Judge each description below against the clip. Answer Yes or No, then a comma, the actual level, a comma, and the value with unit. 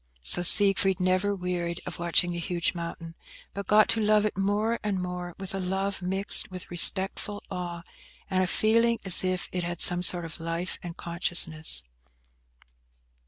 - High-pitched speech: No, medium, 180 Hz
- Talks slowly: No, average, 165 wpm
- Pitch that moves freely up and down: No, narrow, 2.4 semitones